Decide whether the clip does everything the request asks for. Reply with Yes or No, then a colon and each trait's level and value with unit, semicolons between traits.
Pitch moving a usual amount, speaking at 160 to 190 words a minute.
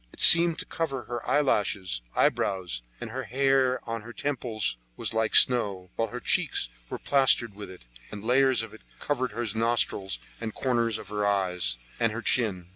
Yes: average, 4.2 semitones; average, 175 wpm